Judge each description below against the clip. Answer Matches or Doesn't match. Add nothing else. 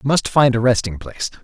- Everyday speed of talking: Doesn't match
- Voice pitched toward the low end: Matches